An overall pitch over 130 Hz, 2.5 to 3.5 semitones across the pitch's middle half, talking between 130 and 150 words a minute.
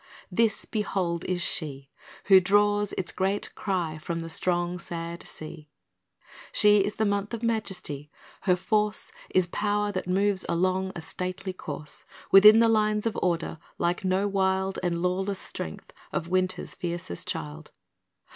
Yes: medium, 185 Hz; average, 3.0 semitones; average, 145 wpm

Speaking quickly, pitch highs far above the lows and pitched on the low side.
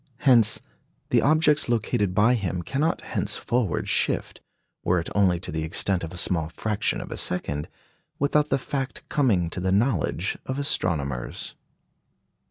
No: average, 150 wpm; wide, 7.0 semitones; low, 100 Hz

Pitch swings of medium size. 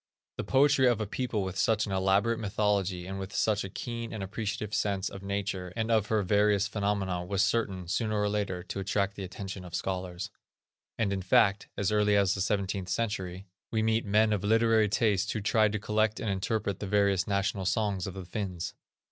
No: narrow, 2.1 semitones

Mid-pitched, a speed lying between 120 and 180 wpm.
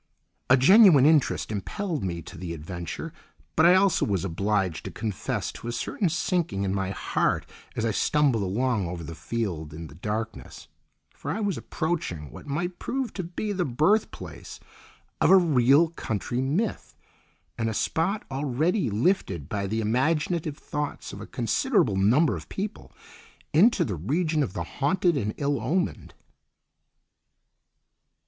No: low, 130 Hz; average, 155 wpm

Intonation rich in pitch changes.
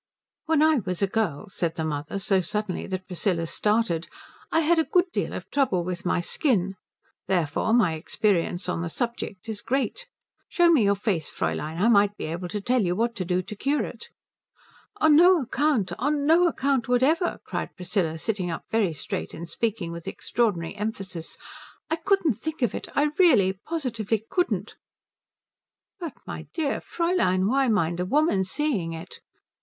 Yes: wide, 8.0 semitones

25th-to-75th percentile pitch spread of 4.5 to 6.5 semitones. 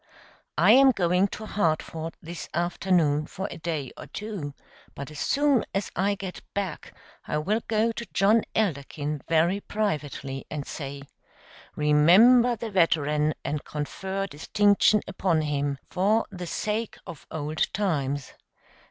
Yes: wide, 5.5 semitones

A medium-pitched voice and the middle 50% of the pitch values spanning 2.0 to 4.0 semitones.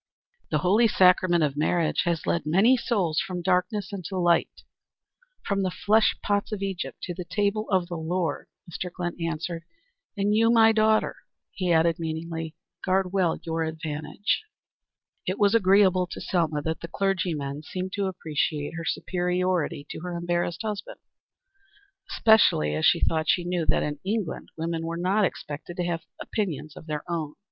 Yes: medium, 175 Hz; average, 3.2 semitones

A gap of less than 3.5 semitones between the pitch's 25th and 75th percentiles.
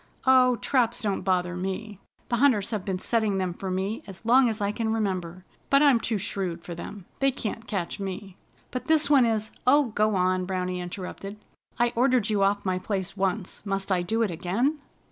No: average, 4.0 semitones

